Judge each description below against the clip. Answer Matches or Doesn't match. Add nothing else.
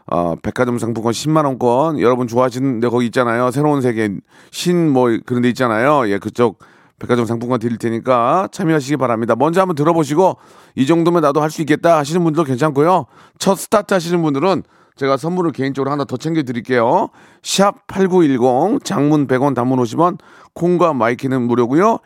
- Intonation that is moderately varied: Matches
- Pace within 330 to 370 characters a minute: Doesn't match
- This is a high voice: Doesn't match